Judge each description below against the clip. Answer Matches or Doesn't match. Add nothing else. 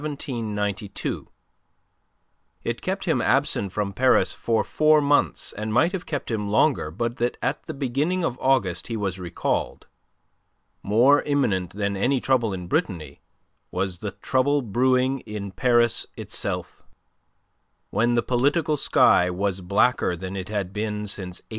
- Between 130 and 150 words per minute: Matches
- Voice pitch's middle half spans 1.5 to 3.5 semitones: Doesn't match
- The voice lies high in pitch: Doesn't match